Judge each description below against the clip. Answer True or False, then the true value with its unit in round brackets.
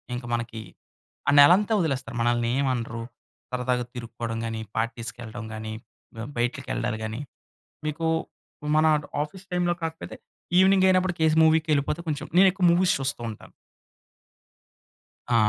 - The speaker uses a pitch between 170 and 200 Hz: False (130 Hz)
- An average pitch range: False (5.9 semitones)